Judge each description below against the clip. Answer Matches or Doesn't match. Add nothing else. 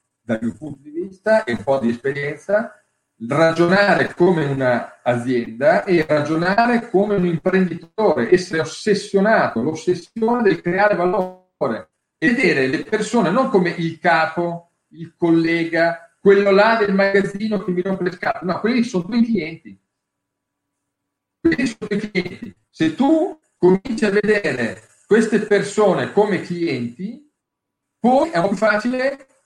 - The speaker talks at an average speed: Matches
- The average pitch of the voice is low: Doesn't match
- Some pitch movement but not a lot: Matches